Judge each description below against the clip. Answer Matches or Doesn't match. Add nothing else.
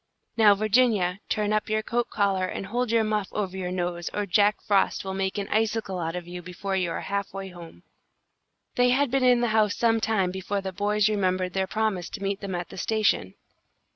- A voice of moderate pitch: Doesn't match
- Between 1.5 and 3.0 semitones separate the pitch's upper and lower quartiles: Matches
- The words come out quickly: Matches